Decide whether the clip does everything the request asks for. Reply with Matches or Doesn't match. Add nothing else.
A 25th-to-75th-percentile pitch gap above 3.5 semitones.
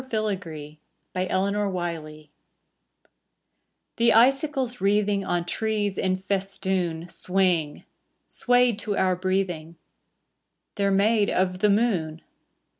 Doesn't match